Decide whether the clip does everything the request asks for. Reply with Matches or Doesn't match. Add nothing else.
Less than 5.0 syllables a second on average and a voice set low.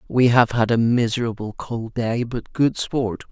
Matches